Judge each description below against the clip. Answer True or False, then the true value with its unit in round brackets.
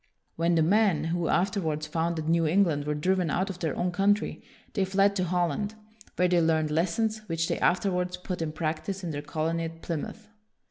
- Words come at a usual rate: True (190 wpm)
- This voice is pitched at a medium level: True (170 Hz)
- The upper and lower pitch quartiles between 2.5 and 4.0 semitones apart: True (2.9 semitones)